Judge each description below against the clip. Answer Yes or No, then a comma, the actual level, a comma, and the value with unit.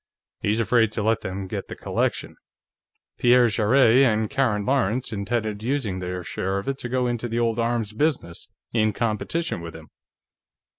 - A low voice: Yes, low, 115 Hz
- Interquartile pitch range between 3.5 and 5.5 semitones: No, average, 3.1 semitones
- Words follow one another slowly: No, average, 165 wpm